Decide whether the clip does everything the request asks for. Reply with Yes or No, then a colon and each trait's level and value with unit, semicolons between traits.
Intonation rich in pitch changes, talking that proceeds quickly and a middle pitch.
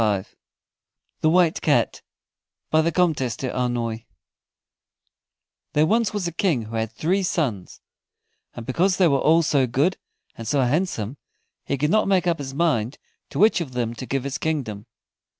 No: wide, 5.9 semitones; average, 160 wpm; medium, 145 Hz